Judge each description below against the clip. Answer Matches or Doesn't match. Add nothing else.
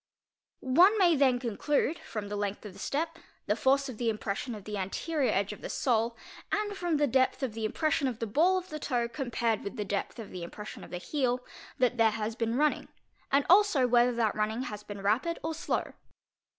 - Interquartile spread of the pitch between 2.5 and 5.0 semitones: Doesn't match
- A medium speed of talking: Doesn't match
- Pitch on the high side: Matches